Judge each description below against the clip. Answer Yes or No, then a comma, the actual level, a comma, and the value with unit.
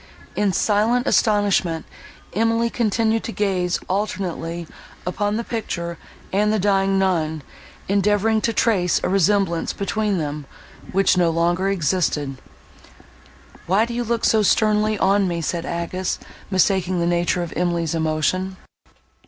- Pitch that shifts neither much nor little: Yes, average, 3.5 semitones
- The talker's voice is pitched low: No, high, 190 Hz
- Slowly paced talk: Yes, slow, 130 wpm